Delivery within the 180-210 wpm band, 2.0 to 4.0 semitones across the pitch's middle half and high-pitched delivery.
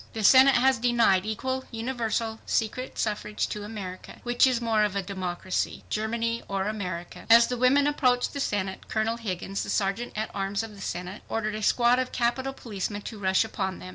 Yes: average, 190 wpm; average, 3.5 semitones; high, 220 Hz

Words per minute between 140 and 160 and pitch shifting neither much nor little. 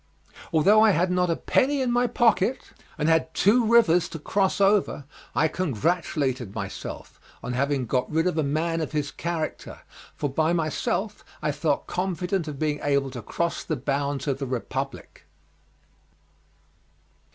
Yes: average, 155 wpm; average, 4.6 semitones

